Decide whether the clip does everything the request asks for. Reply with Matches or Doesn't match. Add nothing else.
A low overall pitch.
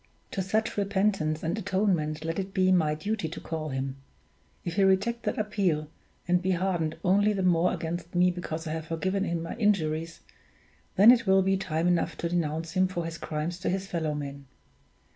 Doesn't match